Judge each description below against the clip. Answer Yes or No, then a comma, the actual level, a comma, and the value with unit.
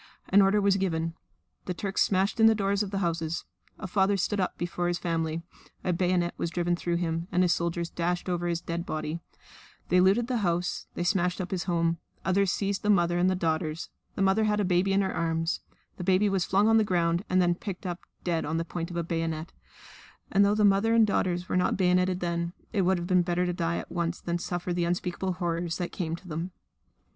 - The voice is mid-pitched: Yes, medium, 180 Hz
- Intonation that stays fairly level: Yes, narrow, 2.2 semitones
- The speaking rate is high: Yes, fast, 230 wpm